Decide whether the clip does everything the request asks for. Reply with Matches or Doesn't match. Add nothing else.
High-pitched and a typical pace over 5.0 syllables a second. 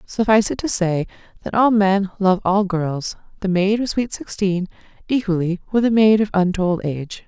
Doesn't match